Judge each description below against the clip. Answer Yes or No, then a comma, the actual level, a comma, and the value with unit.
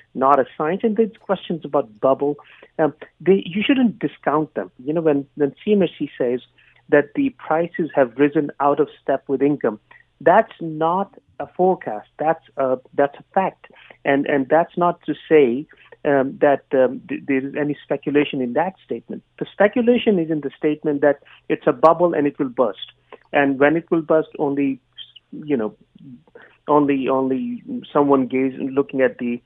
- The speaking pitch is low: No, medium, 150 Hz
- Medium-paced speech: Yes, average, 170 wpm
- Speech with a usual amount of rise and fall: Yes, average, 3.8 semitones